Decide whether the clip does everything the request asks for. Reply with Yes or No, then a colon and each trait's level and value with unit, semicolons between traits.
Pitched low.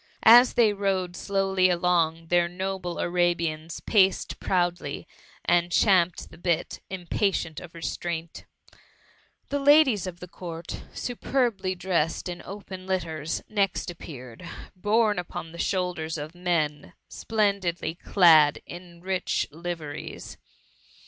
No: medium, 175 Hz